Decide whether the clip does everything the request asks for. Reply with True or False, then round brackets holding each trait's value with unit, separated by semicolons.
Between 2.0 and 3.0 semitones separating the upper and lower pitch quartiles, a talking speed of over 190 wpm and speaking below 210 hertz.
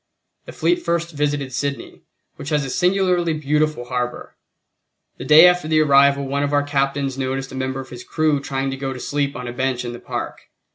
True (2.5 semitones; 205 wpm; 140 Hz)